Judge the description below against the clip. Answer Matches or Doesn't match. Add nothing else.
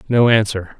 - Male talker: Matches